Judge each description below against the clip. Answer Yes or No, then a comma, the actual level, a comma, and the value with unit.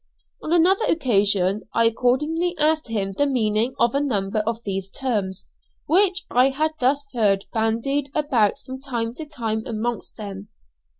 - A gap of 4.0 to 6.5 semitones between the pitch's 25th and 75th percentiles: Yes, average, 5.2 semitones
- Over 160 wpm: No, average, 155 wpm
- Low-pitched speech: No, high, 240 Hz